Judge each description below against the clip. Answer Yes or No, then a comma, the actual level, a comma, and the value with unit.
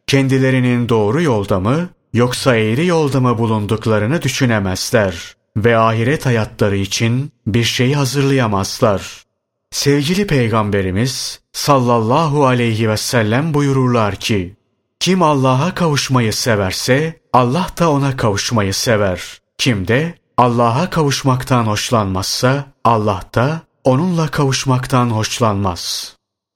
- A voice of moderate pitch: No, low, 125 Hz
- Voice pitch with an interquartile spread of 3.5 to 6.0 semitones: Yes, average, 4.1 semitones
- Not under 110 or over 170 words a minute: No, average, 100 wpm